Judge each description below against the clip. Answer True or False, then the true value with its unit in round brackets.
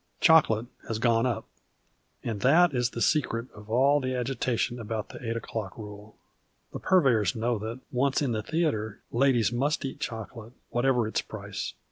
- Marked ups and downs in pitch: False (3.2 semitones)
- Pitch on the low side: True (120 Hz)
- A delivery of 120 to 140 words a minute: False (170 wpm)